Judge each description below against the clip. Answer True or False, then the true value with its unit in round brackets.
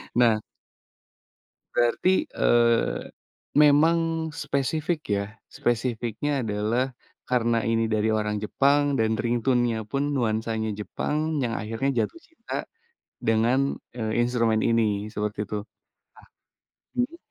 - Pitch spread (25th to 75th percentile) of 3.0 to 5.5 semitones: True (4.0 semitones)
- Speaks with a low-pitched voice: True (115 Hz)